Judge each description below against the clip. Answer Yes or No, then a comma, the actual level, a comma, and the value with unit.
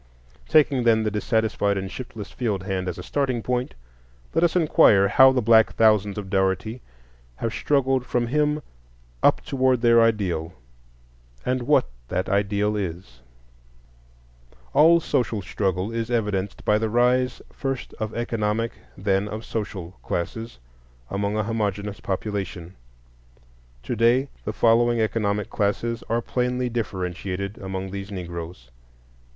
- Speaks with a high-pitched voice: No, low, 110 Hz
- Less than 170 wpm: Yes, slow, 135 wpm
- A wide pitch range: No, average, 3.6 semitones